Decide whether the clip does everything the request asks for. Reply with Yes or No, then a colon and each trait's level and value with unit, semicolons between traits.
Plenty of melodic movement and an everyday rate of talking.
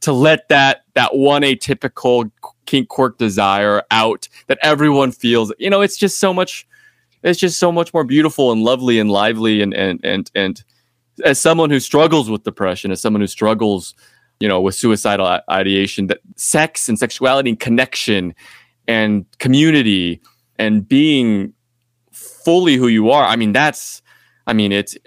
Yes: wide, 5.8 semitones; average, 165 wpm